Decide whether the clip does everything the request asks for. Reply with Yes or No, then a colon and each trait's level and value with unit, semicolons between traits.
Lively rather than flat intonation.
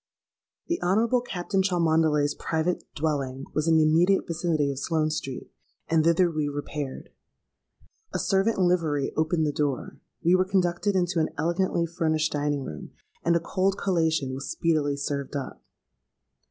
No: average, 3.2 semitones